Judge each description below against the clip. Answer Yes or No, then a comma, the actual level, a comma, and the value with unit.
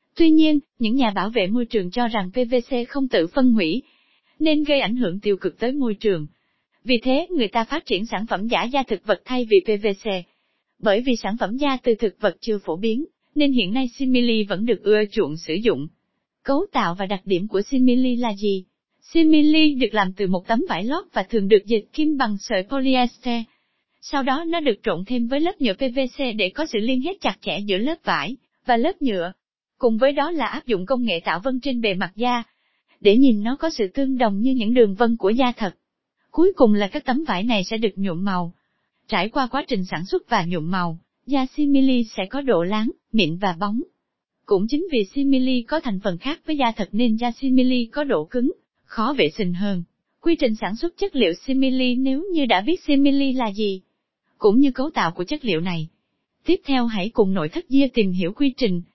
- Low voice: No, high, 240 Hz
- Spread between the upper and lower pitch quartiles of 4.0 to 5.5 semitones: Yes, average, 5.0 semitones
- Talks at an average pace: Yes, average, 225 wpm